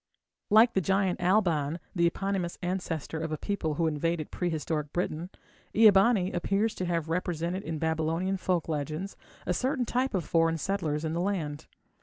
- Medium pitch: Yes, medium, 175 Hz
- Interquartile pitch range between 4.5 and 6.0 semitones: No, average, 3.3 semitones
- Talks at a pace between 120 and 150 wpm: No, average, 165 wpm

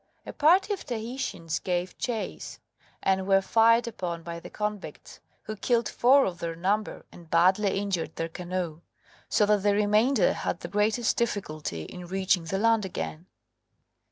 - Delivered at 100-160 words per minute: Yes, average, 155 wpm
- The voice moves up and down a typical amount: Yes, average, 4.2 semitones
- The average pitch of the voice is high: Yes, high, 195 Hz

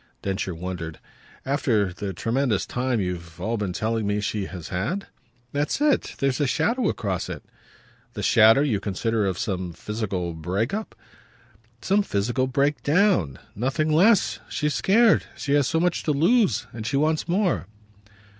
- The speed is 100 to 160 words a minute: Yes, average, 155 wpm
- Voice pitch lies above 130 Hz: No, low, 115 Hz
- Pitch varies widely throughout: Yes, wide, 7.7 semitones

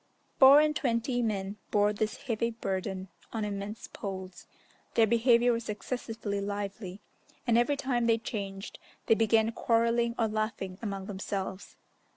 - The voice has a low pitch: No, high, 220 Hz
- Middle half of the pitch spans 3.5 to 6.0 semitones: No, average, 2.7 semitones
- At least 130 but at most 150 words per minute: Yes, average, 140 wpm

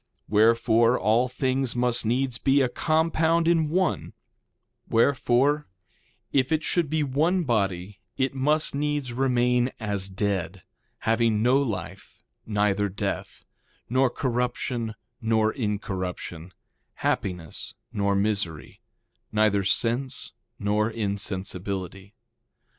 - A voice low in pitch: Yes, low, 115 Hz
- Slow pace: Yes, slow, 105 wpm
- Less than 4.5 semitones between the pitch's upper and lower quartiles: No, average, 4.8 semitones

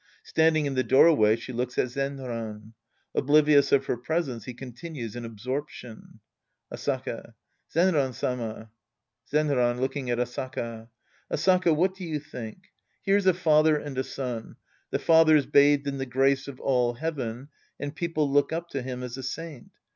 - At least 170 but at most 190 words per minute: No, average, 155 wpm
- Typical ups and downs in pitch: Yes, average, 3.8 semitones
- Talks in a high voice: No, low, 135 Hz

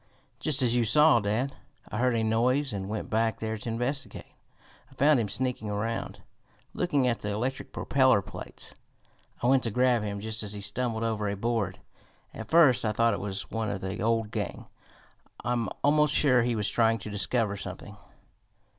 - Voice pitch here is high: No, low, 115 Hz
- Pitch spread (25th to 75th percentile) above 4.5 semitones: No, average, 3.4 semitones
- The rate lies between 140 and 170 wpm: No, average, 185 wpm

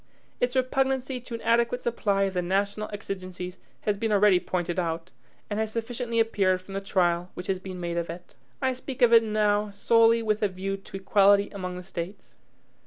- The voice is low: No, high, 200 Hz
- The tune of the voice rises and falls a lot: No, average, 3.7 semitones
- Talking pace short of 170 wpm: No, average, 195 wpm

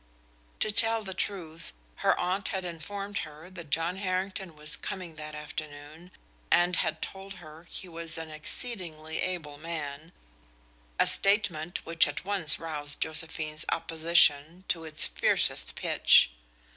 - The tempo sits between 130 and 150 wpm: Yes, slow, 135 wpm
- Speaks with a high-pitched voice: No, medium, 165 Hz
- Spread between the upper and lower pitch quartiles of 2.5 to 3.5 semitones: Yes, average, 3.2 semitones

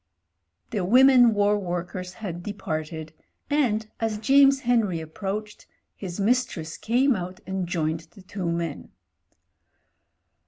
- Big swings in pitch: No, average, 4.7 semitones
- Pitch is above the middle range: Yes, high, 195 Hz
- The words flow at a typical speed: No, slow, 115 wpm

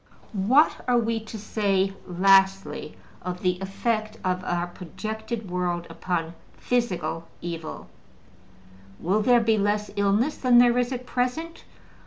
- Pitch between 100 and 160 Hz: No, high, 205 Hz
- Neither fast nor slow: No, slow, 130 wpm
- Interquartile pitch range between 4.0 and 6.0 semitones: Yes, average, 4.6 semitones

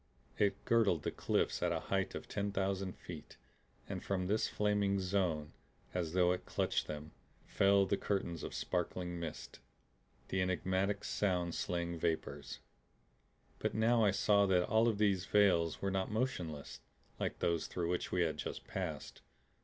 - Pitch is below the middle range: Yes, very low, 95 Hz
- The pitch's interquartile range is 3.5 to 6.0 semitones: No, average, 2.7 semitones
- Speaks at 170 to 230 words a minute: No, average, 160 wpm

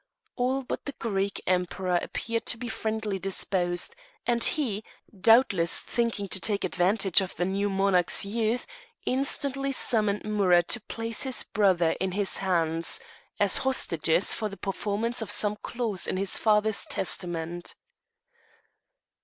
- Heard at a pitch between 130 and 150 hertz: No, high, 200 Hz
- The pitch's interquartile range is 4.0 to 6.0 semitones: No, average, 3.6 semitones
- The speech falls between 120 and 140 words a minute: Yes, slow, 135 wpm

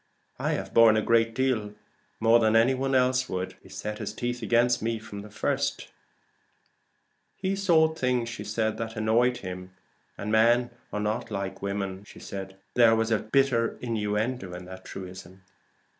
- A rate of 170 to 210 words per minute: No, average, 160 wpm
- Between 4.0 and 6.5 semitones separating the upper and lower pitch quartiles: No, average, 3.1 semitones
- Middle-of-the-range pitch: No, low, 115 Hz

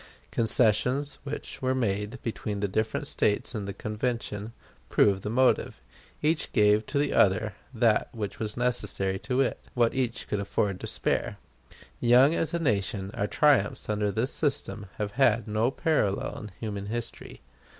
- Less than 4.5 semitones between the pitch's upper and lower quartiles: Yes, average, 3.5 semitones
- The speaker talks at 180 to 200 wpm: No, average, 155 wpm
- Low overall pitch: Yes, low, 110 Hz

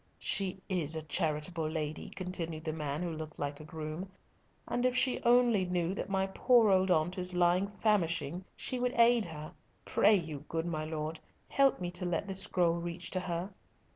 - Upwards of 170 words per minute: Yes, average, 190 wpm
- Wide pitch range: No, average, 3.5 semitones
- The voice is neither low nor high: Yes, medium, 175 Hz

